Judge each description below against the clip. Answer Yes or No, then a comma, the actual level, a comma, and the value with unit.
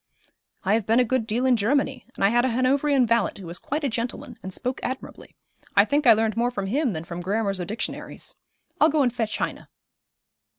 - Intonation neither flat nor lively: Yes, average, 3.8 semitones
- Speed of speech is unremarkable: No, fast, 220 wpm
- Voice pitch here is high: Yes, high, 235 Hz